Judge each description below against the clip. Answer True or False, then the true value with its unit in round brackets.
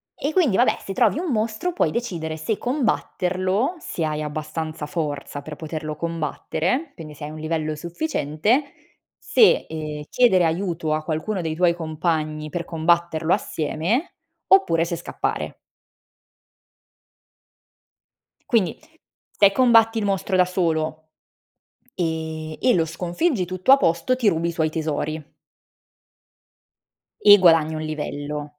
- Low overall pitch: False (165 Hz)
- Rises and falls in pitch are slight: False (4.5 semitones)